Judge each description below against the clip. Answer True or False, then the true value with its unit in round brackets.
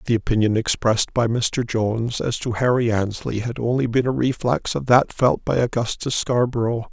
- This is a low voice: True (115 Hz)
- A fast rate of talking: False (180 wpm)